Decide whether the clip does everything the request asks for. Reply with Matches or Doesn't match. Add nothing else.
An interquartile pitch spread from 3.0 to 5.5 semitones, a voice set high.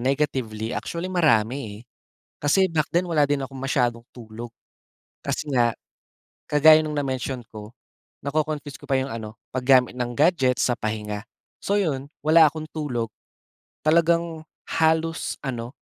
Doesn't match